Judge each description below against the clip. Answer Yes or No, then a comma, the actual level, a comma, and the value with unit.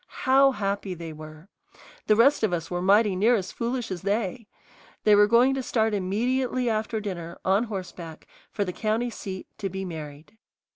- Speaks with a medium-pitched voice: No, high, 205 Hz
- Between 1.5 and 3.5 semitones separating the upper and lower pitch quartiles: No, average, 4.1 semitones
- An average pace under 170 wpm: No, average, 180 wpm